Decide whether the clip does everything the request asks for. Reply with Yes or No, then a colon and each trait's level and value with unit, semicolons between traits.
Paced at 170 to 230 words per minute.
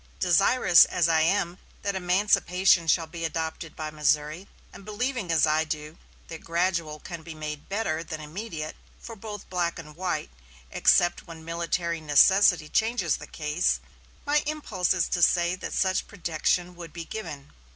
No: average, 160 wpm